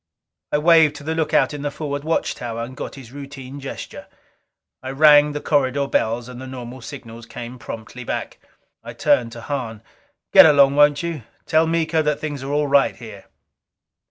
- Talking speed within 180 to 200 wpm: Yes, average, 185 wpm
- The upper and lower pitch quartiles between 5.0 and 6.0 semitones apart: No, average, 3.1 semitones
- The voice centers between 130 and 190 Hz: Yes, medium, 140 Hz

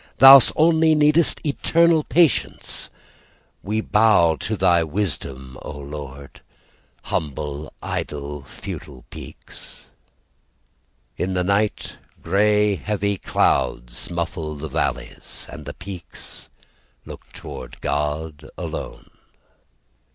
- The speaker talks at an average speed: No, slow, 95 wpm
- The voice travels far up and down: Yes, wide, 6.5 semitones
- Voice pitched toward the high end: No, very low, 90 Hz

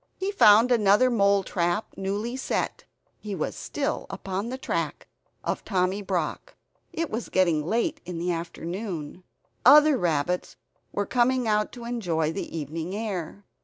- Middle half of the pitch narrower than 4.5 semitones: No, average, 5.3 semitones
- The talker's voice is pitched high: Yes, high, 200 Hz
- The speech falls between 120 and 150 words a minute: Yes, average, 145 wpm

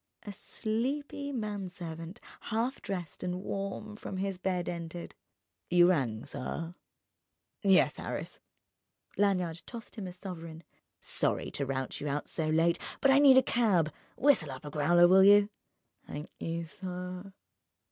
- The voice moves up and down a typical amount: Yes, average, 3.8 semitones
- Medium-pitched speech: Yes, medium, 180 Hz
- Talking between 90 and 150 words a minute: Yes, average, 140 wpm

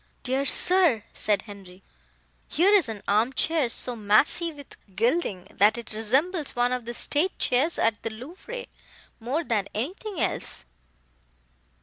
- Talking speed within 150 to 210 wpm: No, average, 140 wpm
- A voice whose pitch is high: Yes, very high, 250 Hz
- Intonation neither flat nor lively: No, wide, 7.2 semitones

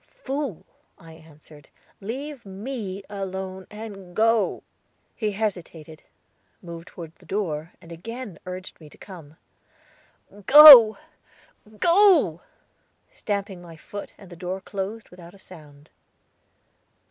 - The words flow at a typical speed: No, slow, 110 wpm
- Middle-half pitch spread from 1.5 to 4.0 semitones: No, average, 4.4 semitones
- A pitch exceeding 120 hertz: Yes, high, 190 Hz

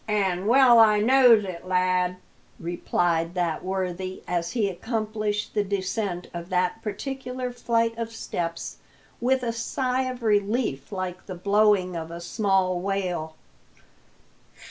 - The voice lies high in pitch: Yes, high, 200 Hz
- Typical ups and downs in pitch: Yes, average, 4.1 semitones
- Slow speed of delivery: Yes, slow, 130 wpm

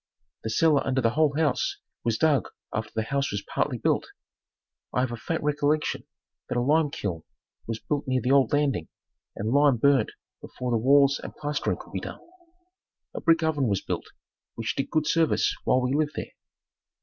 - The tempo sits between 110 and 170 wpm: No, average, 185 wpm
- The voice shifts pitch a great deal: No, average, 4.0 semitones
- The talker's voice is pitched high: No, medium, 140 Hz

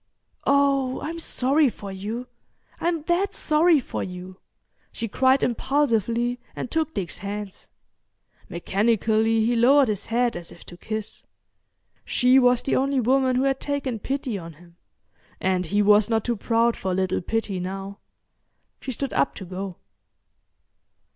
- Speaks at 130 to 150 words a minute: Yes, average, 145 wpm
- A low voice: No, high, 230 Hz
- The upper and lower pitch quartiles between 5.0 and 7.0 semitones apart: Yes, wide, 5.4 semitones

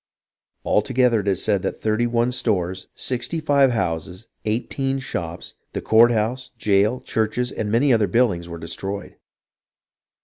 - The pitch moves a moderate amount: Yes, average, 4.2 semitones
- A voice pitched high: No, low, 110 Hz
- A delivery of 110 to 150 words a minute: Yes, average, 145 wpm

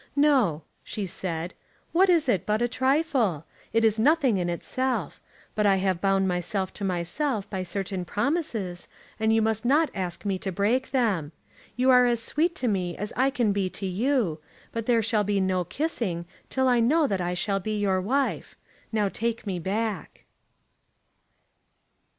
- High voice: Yes, high, 210 Hz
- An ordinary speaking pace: Yes, average, 175 wpm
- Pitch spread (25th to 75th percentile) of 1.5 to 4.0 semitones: No, average, 5.1 semitones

